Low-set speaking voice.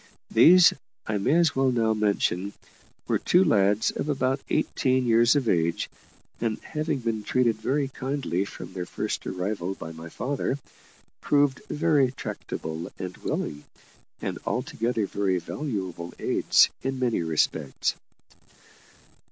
Yes: low, 115 Hz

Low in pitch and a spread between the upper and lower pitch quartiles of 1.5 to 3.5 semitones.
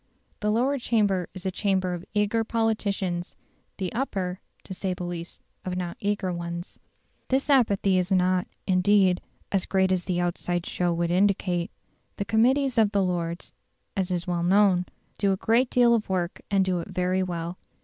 No: medium, 185 Hz; narrow, 2.6 semitones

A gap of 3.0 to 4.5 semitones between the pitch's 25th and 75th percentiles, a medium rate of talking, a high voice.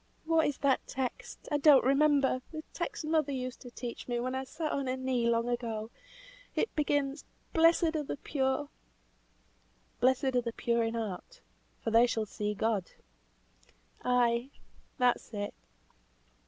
Yes: average, 3.7 semitones; average, 155 wpm; very high, 260 Hz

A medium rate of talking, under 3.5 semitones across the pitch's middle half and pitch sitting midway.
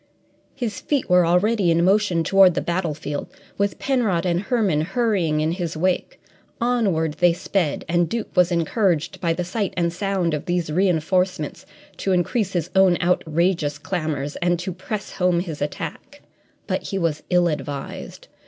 Yes: average, 160 wpm; average, 2.9 semitones; medium, 175 Hz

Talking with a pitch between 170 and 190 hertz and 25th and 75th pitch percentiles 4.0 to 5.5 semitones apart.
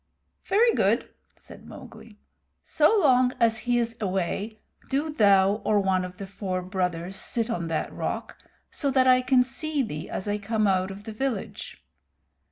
No: high, 215 Hz; average, 5.0 semitones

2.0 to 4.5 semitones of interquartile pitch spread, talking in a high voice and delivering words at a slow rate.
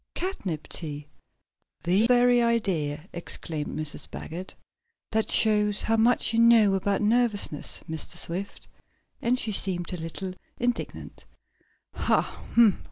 No: wide, 5.5 semitones; high, 200 Hz; slow, 115 wpm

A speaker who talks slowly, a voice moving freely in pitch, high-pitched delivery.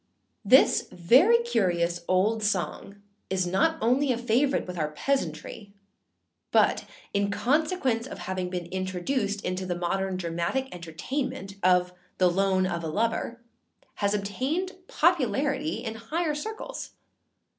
Yes: slow, 125 wpm; wide, 6.7 semitones; high, 200 Hz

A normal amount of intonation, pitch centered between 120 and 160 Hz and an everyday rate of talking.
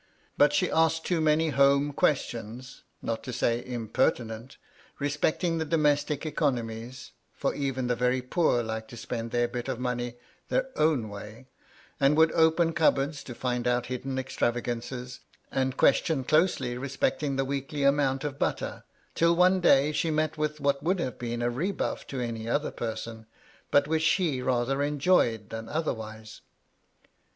Yes: average, 4.0 semitones; low, 135 Hz; average, 160 wpm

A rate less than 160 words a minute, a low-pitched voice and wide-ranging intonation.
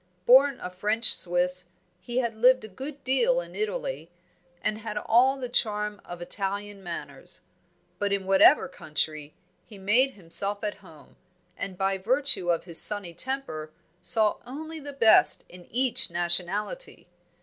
No: average, 150 wpm; high, 210 Hz; wide, 6.1 semitones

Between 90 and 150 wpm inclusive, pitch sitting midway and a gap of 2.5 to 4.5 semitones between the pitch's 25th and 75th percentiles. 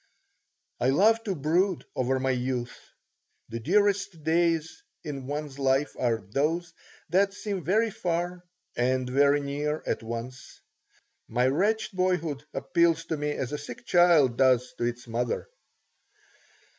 No: slow, 135 wpm; medium, 150 Hz; average, 5.3 semitones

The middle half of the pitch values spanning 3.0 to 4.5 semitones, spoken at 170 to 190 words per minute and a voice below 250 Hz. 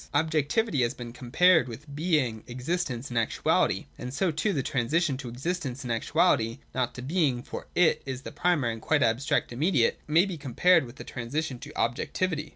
No: average, 5.0 semitones; average, 180 wpm; medium, 140 Hz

